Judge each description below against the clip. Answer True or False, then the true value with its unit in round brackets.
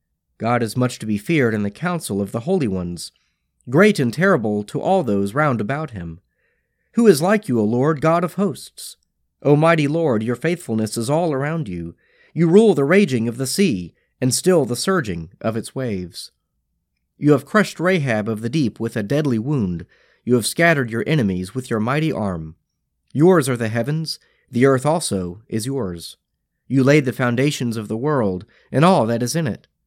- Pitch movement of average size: False (6.7 semitones)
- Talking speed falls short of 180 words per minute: False (195 wpm)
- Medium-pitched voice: False (125 Hz)